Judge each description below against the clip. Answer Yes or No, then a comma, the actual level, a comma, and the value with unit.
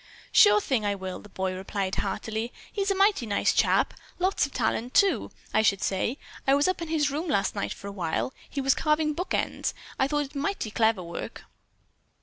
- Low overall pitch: No, very high, 260 Hz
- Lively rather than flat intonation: Yes, wide, 7.6 semitones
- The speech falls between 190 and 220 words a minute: Yes, fast, 205 wpm